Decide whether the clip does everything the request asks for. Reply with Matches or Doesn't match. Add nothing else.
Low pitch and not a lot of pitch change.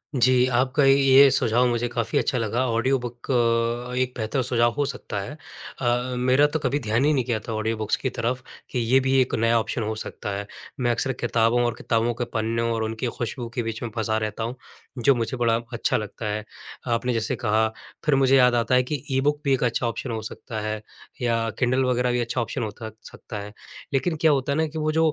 Matches